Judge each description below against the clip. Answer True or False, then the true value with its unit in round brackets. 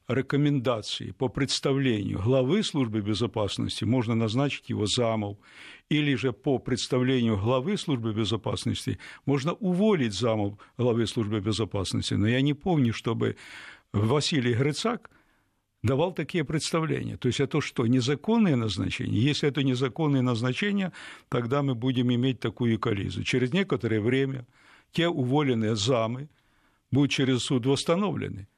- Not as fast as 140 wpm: True (125 wpm)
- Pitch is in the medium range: False (130 Hz)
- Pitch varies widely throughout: False (3.7 semitones)